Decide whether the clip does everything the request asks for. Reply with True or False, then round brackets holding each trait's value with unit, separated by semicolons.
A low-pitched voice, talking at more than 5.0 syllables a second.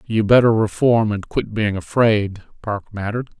False (110 Hz; 4.8 syllables/s)